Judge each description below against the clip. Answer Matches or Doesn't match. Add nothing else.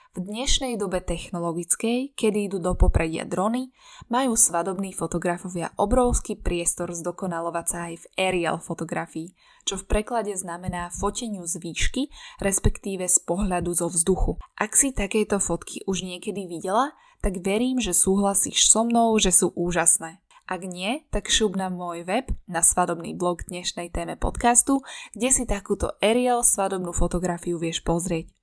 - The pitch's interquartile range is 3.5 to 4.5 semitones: Matches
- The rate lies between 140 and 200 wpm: Matches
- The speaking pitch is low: Doesn't match